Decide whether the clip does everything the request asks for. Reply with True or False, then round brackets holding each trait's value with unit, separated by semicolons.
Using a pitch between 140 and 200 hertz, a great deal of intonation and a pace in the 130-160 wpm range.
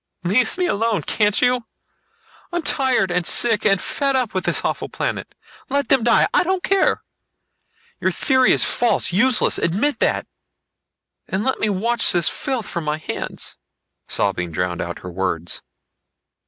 False (220 Hz; 7.3 semitones; 155 wpm)